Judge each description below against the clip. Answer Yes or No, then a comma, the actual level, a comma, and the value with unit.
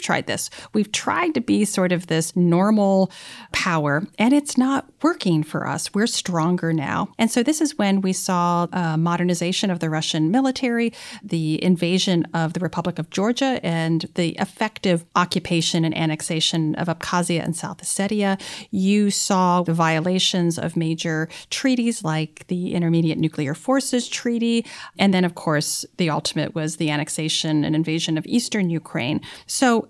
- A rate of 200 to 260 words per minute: No, average, 155 wpm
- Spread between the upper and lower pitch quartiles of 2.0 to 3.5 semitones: No, average, 4.1 semitones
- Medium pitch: Yes, medium, 180 Hz